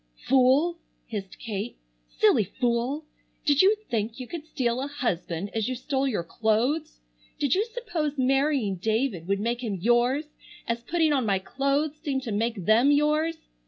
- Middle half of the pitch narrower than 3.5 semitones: No, average, 5.1 semitones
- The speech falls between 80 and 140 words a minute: No, average, 160 wpm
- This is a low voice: No, very high, 255 Hz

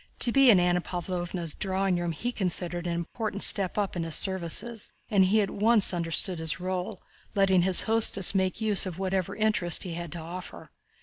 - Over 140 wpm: Yes, average, 190 wpm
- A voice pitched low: No, medium, 185 Hz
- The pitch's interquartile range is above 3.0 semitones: No, average, 2.7 semitones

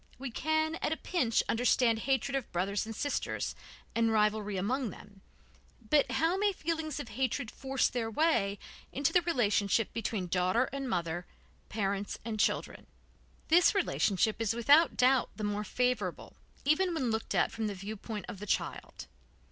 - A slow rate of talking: No, average, 160 wpm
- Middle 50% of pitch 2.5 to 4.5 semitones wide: No, average, 5.2 semitones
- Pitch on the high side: Yes, high, 230 Hz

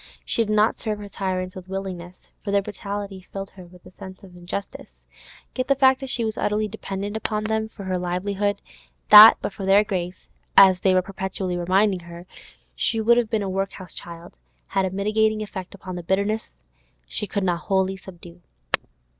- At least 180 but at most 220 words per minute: Yes, average, 185 wpm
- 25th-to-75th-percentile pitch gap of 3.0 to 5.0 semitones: No, narrow, 2.4 semitones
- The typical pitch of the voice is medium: No, high, 195 Hz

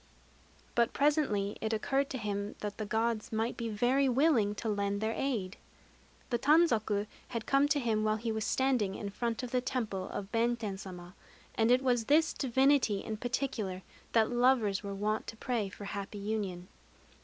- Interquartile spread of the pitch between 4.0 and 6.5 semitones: No, average, 3.6 semitones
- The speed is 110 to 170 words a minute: No, average, 180 wpm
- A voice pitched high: Yes, high, 225 Hz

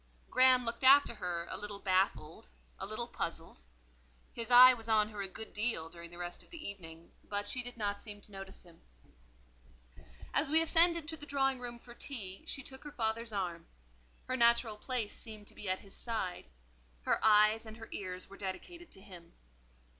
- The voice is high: Yes, high, 220 Hz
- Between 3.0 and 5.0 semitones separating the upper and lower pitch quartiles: Yes, average, 4.7 semitones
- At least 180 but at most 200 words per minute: Yes, average, 190 wpm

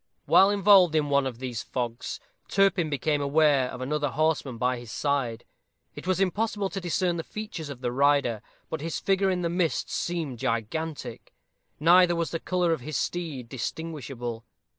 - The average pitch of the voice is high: No, medium, 155 Hz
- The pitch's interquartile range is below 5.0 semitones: No, average, 5.3 semitones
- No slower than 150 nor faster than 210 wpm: Yes, average, 170 wpm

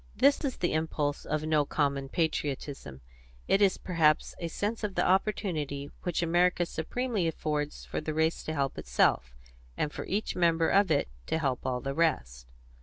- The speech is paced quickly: No, average, 175 wpm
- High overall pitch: No, medium, 160 Hz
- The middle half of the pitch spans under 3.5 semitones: No, average, 4.0 semitones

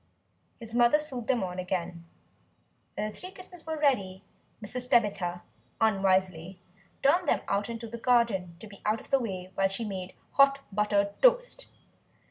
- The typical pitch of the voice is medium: No, high, 215 Hz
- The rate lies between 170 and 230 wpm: No, average, 160 wpm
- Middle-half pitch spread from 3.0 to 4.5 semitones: No, average, 5.0 semitones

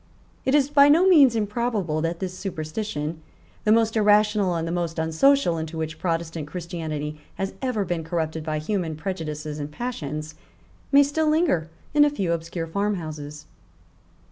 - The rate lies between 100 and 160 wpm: Yes, average, 155 wpm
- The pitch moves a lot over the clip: Yes, wide, 5.7 semitones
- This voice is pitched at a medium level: Yes, medium, 170 Hz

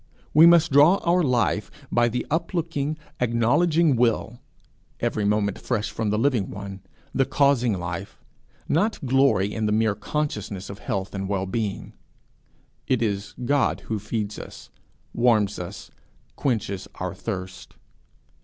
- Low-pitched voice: Yes, low, 115 Hz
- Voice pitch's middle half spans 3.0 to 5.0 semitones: No, wide, 5.6 semitones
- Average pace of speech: No, slow, 130 wpm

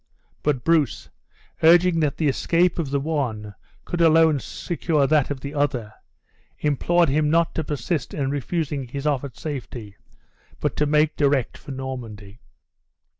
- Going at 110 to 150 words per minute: Yes, average, 145 wpm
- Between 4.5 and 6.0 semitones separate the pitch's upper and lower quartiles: No, average, 3.3 semitones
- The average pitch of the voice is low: No, medium, 145 Hz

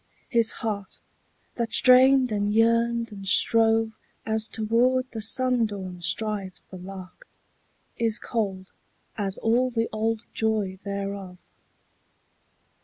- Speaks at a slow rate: Yes, slow, 110 wpm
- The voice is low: No, high, 220 Hz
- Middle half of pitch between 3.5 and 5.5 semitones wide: No, average, 2.7 semitones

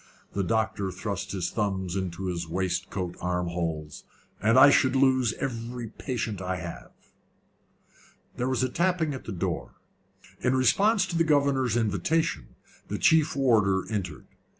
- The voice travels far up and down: Yes, wide, 6.2 semitones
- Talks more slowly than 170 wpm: Yes, average, 145 wpm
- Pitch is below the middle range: Yes, low, 110 Hz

